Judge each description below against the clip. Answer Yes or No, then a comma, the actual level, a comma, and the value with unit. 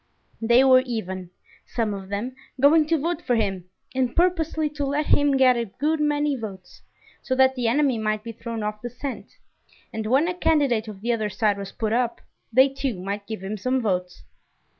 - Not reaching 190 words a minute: No, average, 200 wpm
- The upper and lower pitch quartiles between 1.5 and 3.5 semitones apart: No, average, 4.7 semitones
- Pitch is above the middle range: Yes, high, 240 Hz